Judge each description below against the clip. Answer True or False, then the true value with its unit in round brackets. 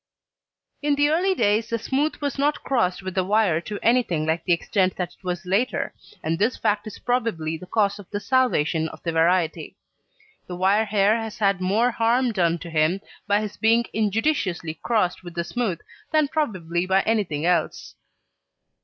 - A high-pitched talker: True (200 Hz)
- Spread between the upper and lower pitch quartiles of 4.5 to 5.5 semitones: True (4.8 semitones)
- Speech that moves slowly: False (180 wpm)